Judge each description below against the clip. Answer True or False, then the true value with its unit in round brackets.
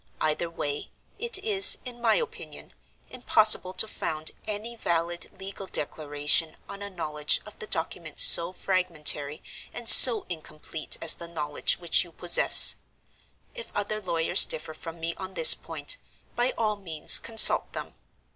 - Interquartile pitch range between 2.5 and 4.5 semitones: False (5.2 semitones)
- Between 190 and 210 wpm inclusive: False (145 wpm)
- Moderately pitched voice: True (175 Hz)